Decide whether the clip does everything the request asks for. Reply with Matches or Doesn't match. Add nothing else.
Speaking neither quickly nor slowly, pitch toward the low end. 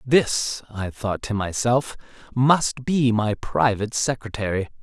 Doesn't match